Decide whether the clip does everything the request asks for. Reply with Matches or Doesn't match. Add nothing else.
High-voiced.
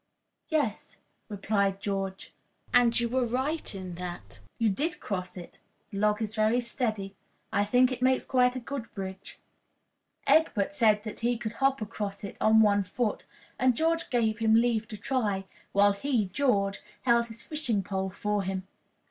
Matches